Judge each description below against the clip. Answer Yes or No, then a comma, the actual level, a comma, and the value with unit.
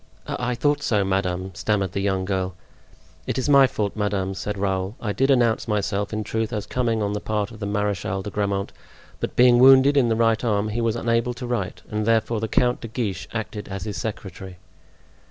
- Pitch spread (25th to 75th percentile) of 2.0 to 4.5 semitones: Yes, average, 3.0 semitones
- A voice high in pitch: No, low, 105 Hz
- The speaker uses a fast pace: Yes, fast, 210 wpm